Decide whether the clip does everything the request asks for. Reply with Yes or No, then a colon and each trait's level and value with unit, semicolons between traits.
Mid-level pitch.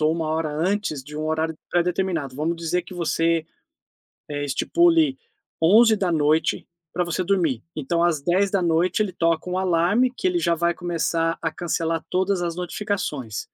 Yes: medium, 170 Hz